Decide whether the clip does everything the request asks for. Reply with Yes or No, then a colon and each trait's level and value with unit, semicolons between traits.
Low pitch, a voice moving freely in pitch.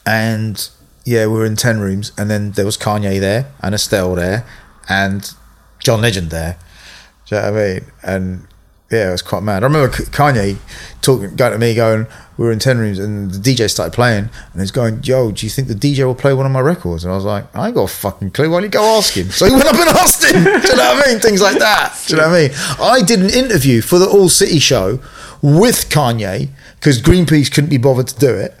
Yes: low, 115 Hz; wide, 5.7 semitones